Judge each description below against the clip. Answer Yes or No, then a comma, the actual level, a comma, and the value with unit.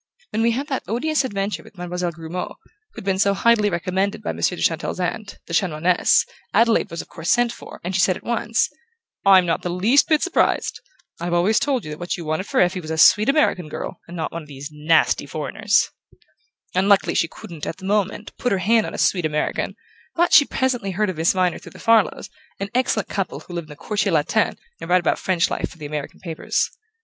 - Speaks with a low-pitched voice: No, medium, 185 Hz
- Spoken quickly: Yes, fast, 225 wpm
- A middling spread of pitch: Yes, average, 4.2 semitones